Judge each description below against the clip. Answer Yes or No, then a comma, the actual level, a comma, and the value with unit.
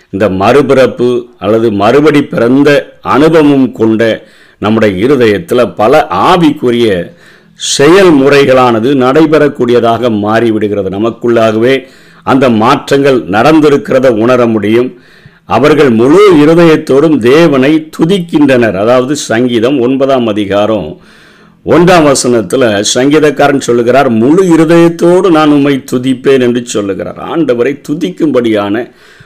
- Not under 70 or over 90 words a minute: Yes, average, 85 wpm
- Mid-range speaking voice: No, low, 125 Hz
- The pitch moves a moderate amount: Yes, average, 4.4 semitones